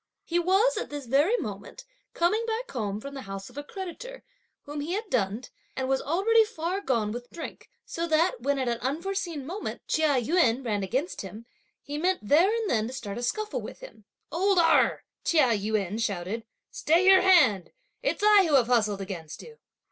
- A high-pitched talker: Yes, very high, 290 Hz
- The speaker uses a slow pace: No, average, 195 wpm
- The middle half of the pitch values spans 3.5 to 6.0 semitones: No, wide, 8.5 semitones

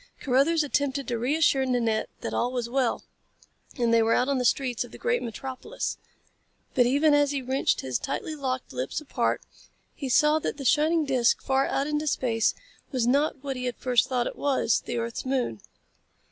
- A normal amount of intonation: Yes, average, 3.0 semitones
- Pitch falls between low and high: No, very high, 260 Hz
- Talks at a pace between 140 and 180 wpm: No, average, 190 wpm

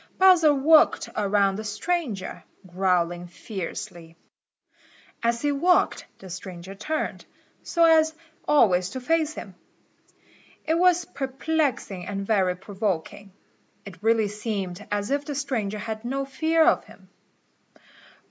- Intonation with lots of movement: Yes, wide, 7.4 semitones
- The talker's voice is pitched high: Yes, high, 215 Hz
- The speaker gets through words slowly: Yes, slow, 120 wpm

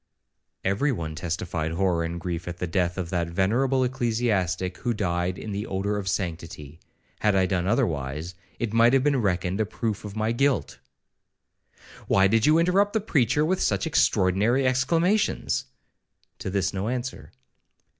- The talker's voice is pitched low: Yes, low, 100 Hz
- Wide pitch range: Yes, wide, 5.9 semitones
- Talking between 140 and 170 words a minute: Yes, average, 155 wpm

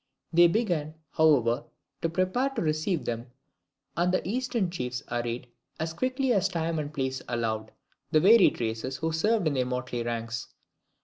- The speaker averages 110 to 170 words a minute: Yes, average, 160 wpm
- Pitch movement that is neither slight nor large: No, wide, 7.1 semitones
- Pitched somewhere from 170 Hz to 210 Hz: No, medium, 155 Hz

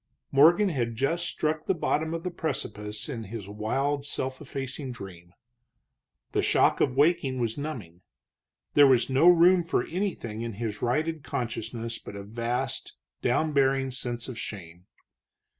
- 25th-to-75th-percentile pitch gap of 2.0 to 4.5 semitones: No, wide, 5.4 semitones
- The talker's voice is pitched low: Yes, low, 130 Hz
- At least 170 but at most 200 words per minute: No, average, 150 wpm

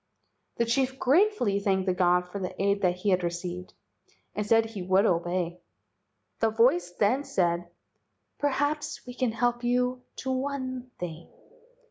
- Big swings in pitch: Yes, wide, 5.9 semitones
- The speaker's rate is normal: Yes, average, 150 wpm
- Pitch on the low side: No, high, 205 Hz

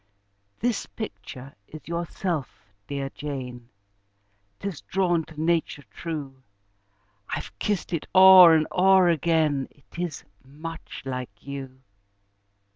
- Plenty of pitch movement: No, average, 4.2 semitones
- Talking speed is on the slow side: Yes, slow, 110 wpm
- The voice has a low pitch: No, medium, 155 Hz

